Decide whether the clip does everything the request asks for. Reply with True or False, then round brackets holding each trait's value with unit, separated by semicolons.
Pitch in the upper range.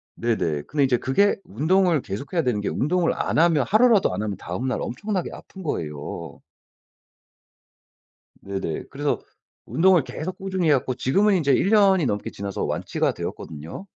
False (145 Hz)